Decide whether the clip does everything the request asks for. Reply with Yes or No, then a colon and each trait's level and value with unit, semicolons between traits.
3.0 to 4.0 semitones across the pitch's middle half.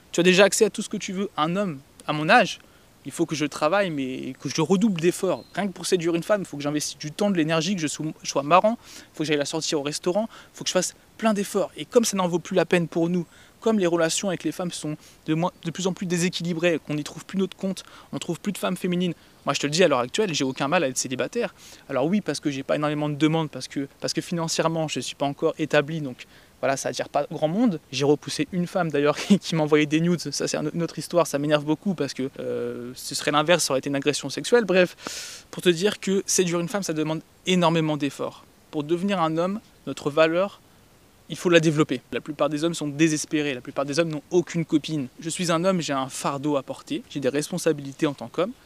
Yes: average, 3.7 semitones